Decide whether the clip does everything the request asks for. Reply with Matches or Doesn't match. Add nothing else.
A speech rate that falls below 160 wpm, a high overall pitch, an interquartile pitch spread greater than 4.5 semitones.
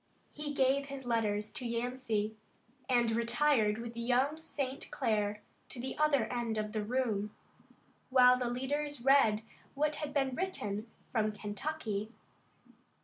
Doesn't match